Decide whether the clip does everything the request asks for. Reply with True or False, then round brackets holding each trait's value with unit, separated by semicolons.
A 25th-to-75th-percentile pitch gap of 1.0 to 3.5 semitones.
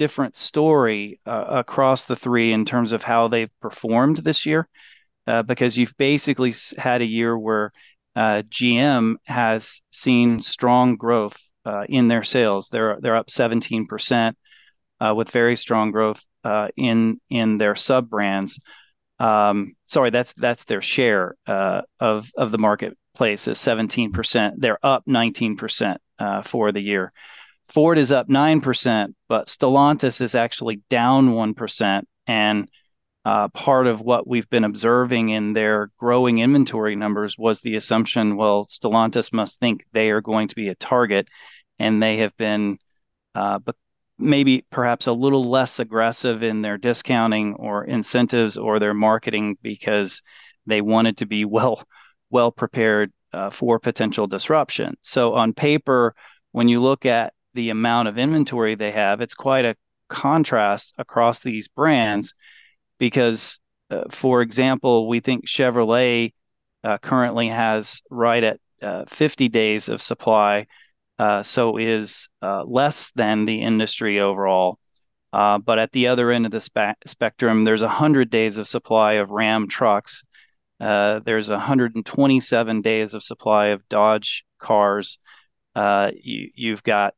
True (2.4 semitones)